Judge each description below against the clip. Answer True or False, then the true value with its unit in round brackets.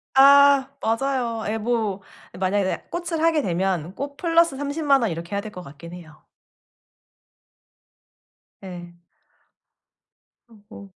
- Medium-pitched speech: False (225 Hz)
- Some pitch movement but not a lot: False (7.1 semitones)